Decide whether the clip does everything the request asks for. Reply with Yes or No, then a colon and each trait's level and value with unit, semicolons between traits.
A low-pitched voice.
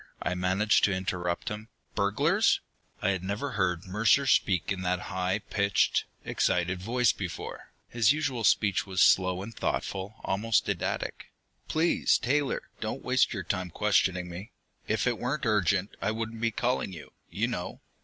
Yes: low, 100 Hz